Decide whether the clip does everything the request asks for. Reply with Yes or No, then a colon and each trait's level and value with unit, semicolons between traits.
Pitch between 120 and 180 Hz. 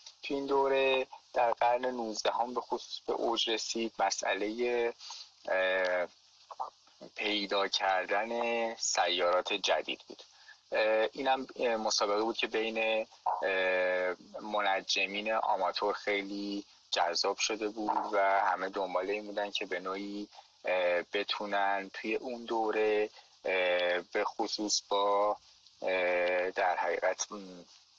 No: low, 105 Hz